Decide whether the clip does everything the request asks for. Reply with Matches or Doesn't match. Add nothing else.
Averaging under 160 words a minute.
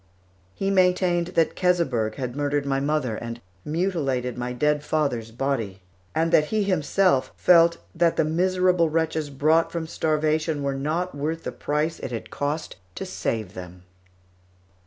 Matches